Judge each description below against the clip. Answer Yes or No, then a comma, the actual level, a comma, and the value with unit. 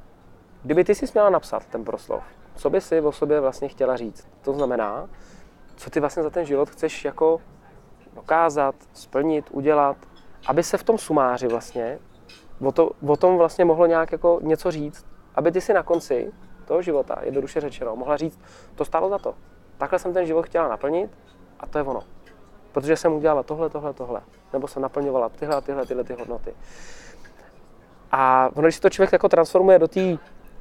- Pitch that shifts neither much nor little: Yes, average, 3.8 semitones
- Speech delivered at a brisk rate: Yes, fast, 180 wpm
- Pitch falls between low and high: Yes, medium, 150 Hz